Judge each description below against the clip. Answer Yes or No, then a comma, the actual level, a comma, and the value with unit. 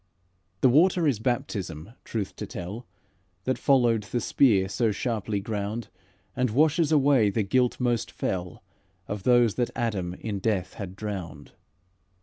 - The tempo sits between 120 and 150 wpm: Yes, average, 140 wpm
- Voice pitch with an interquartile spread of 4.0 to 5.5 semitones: Yes, average, 4.3 semitones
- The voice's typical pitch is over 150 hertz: No, low, 110 Hz